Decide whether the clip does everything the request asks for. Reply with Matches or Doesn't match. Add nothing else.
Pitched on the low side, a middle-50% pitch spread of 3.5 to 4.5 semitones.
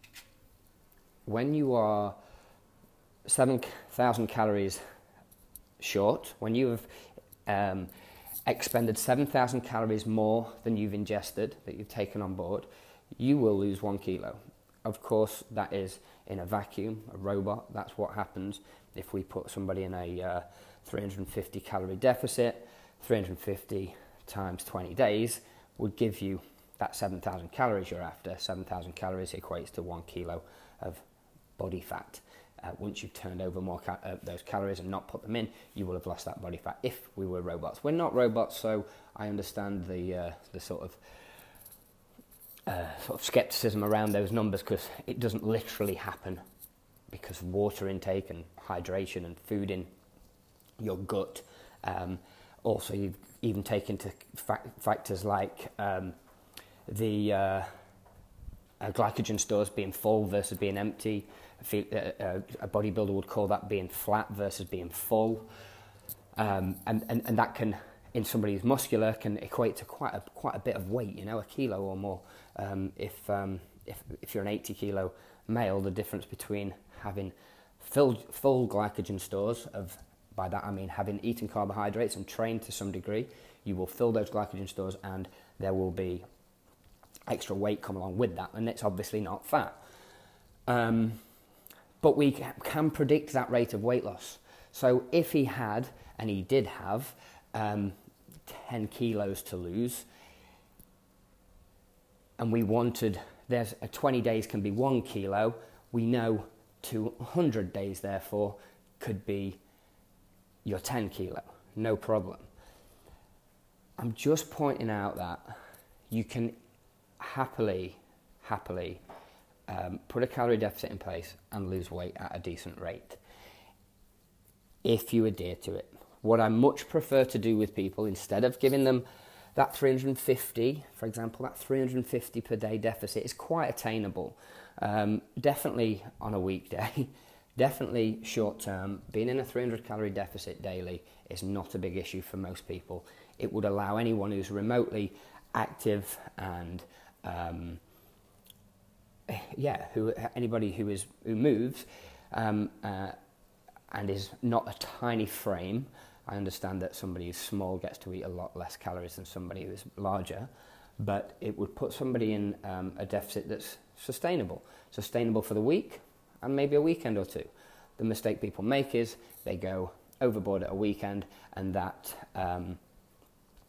Doesn't match